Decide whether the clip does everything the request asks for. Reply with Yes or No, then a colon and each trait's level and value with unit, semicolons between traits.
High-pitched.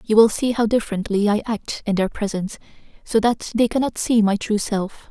Yes: high, 215 Hz